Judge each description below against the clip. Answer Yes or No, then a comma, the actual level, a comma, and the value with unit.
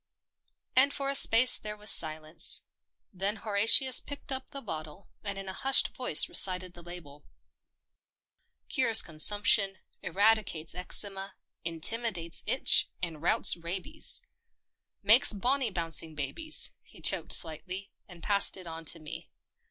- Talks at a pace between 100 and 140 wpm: Yes, slow, 135 wpm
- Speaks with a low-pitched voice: No, high, 195 Hz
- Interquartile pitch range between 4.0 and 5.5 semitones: Yes, average, 5.2 semitones